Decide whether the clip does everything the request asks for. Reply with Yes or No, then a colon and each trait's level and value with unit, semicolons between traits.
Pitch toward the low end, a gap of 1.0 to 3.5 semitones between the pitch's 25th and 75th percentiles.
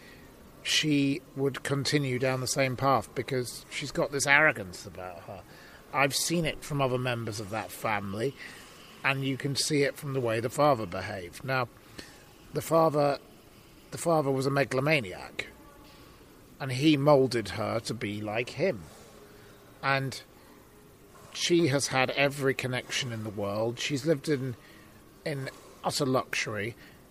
No: low, 130 Hz; average, 4.2 semitones